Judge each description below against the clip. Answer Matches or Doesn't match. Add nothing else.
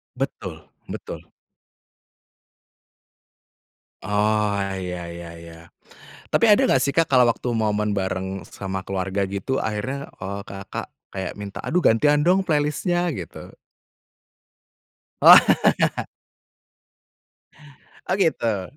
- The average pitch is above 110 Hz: Doesn't match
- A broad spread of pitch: Matches